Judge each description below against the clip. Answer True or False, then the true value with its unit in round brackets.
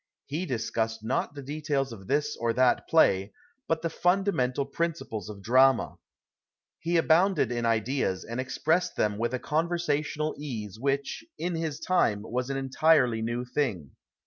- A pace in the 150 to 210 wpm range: True (155 wpm)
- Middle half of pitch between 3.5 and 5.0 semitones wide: False (5.5 semitones)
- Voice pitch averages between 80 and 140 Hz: True (135 Hz)